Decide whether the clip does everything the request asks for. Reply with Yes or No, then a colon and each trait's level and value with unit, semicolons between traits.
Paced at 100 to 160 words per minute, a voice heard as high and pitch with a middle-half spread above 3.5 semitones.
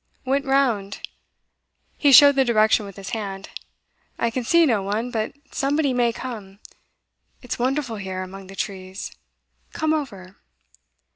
Yes: average, 140 wpm; high, 230 Hz; wide, 5.5 semitones